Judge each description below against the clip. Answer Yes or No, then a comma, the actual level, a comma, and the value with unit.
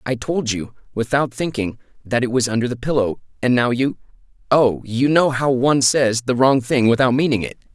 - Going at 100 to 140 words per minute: No, average, 200 wpm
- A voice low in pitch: Yes, low, 125 Hz